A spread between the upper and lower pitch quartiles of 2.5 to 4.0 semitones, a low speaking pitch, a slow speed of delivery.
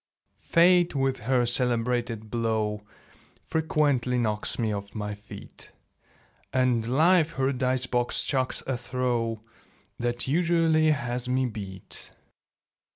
Yes: average, 2.9 semitones; low, 125 Hz; slow, 110 wpm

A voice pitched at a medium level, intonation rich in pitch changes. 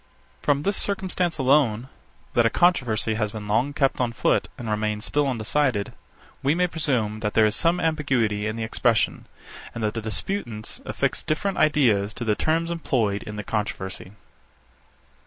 No: low, 120 Hz; wide, 5.9 semitones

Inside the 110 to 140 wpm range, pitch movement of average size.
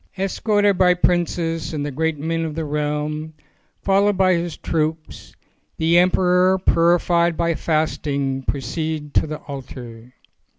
Yes: slow, 135 wpm; average, 3.0 semitones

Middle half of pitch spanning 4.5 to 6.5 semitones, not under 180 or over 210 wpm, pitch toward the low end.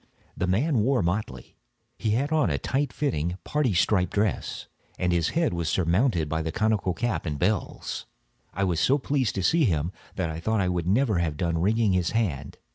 Yes: wide, 5.6 semitones; average, 200 wpm; very low, 95 Hz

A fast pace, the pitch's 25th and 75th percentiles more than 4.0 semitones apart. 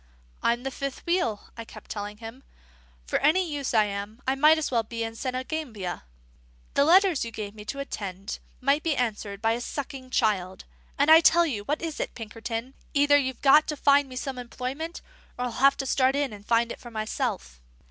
Yes: fast, 210 wpm; average, 4.4 semitones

